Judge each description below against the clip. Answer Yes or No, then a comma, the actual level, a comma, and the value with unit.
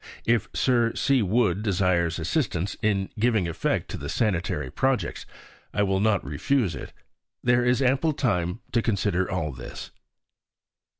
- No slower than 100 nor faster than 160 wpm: Yes, average, 140 wpm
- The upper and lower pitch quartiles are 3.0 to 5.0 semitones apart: No, wide, 5.6 semitones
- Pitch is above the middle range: No, low, 105 Hz